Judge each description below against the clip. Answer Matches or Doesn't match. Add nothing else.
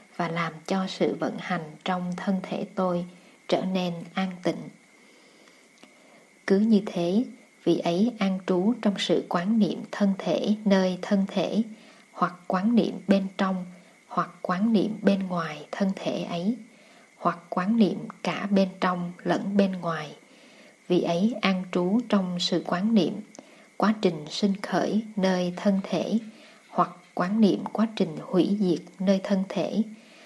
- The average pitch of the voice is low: Doesn't match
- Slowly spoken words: Matches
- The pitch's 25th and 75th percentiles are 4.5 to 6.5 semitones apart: Doesn't match